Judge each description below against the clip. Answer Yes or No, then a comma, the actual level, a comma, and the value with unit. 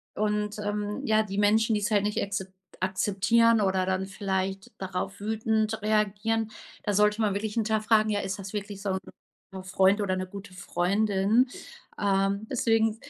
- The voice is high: Yes, high, 205 Hz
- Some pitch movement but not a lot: No, narrow, 2.0 semitones